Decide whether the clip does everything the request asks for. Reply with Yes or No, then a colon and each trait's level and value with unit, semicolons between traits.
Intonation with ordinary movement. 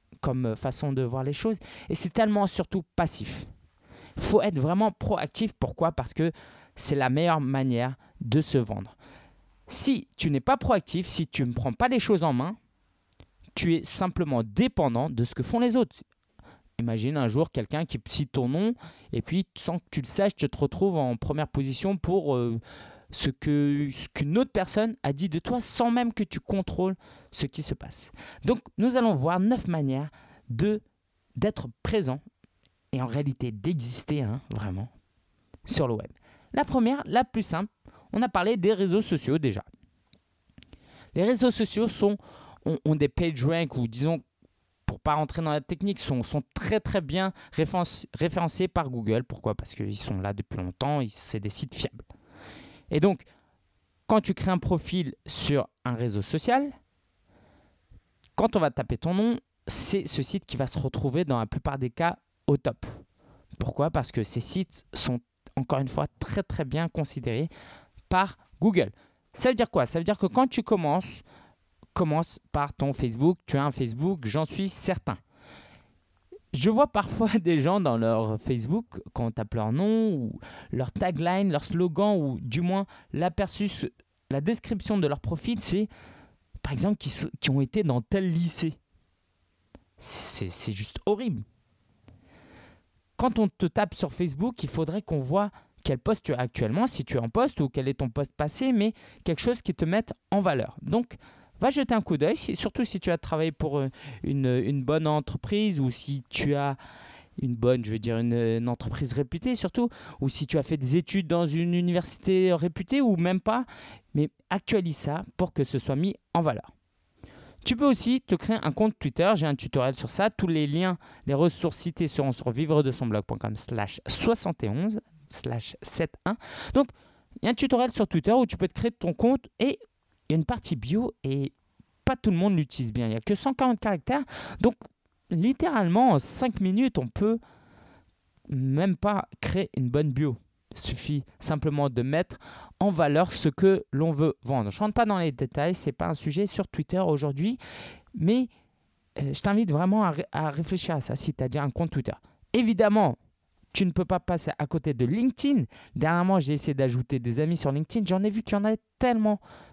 No: wide, 7.3 semitones